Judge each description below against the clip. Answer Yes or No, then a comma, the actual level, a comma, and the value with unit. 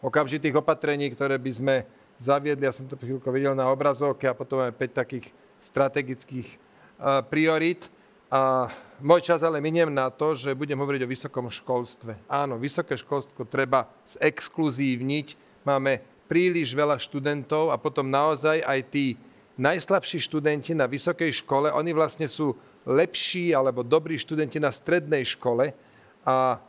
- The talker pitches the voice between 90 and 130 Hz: No, medium, 140 Hz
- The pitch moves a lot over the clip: No, average, 2.8 semitones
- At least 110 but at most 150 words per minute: Yes, average, 140 wpm